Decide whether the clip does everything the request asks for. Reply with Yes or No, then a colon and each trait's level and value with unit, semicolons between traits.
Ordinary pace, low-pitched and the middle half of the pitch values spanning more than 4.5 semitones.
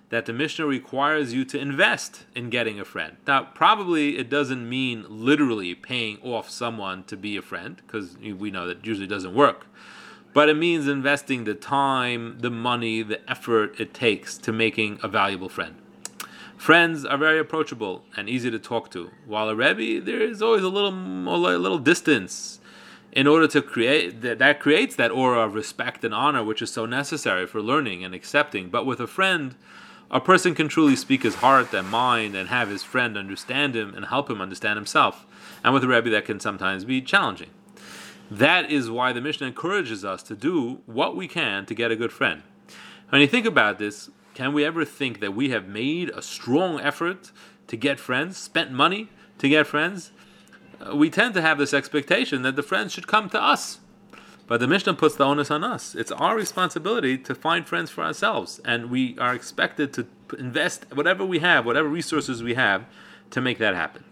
Yes: average, 195 wpm; low, 130 Hz; wide, 5.6 semitones